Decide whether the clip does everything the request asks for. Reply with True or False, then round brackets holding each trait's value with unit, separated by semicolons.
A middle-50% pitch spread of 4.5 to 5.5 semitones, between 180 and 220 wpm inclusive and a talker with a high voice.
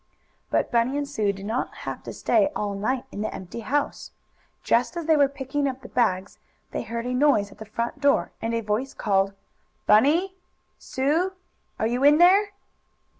True (5.2 semitones; 185 wpm; 250 Hz)